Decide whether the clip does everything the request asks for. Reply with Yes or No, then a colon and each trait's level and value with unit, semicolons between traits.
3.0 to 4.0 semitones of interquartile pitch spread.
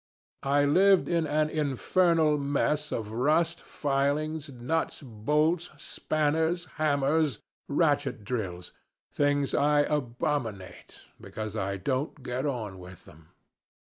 No: average, 4.5 semitones